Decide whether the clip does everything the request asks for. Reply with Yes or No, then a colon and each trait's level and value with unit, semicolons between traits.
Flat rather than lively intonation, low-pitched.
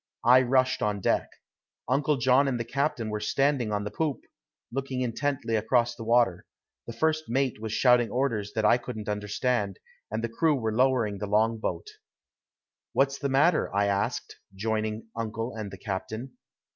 No: average, 3.6 semitones; low, 115 Hz